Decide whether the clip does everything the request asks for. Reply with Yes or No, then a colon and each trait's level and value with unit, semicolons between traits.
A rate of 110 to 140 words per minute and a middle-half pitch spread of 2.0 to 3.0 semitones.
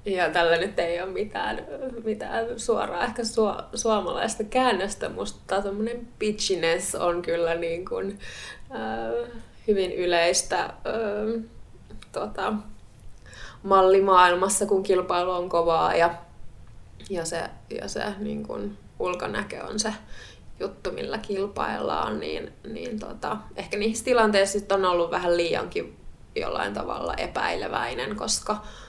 No: average, 115 wpm; average, 4.5 semitones